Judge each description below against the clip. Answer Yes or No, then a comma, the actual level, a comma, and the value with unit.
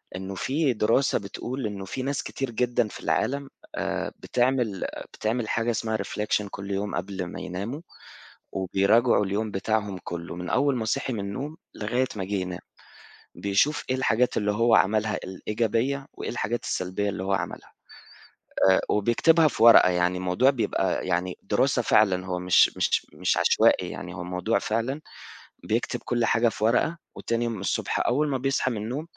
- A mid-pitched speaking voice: No, low, 110 Hz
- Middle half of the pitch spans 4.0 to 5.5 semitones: Yes, average, 4.3 semitones